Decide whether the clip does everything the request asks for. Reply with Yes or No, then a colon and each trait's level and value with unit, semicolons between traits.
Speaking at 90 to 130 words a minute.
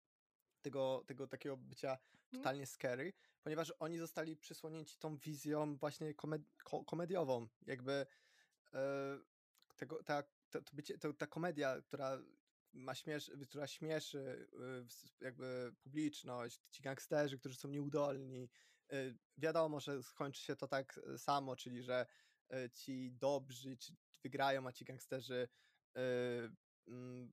Yes: slow, 110 wpm